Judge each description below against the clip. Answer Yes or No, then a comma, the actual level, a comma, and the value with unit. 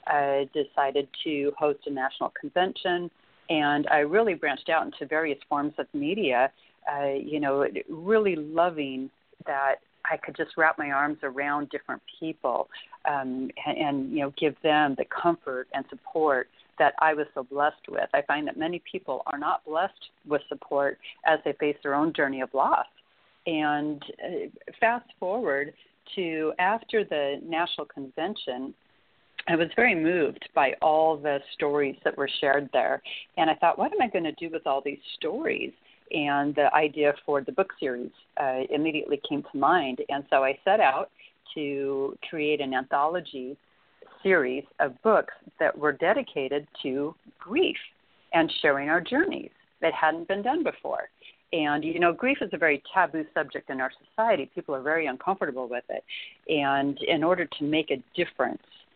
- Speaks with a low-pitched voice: No, medium, 150 Hz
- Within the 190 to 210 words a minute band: No, average, 165 wpm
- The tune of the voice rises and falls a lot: No, average, 3.2 semitones